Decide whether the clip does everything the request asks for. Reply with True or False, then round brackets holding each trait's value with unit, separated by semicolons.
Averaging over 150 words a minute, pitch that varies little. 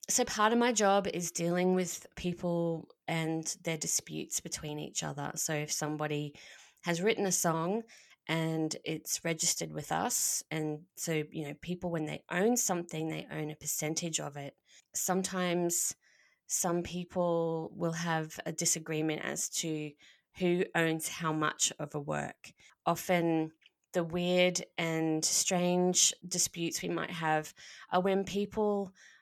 False (145 wpm; 2.3 semitones)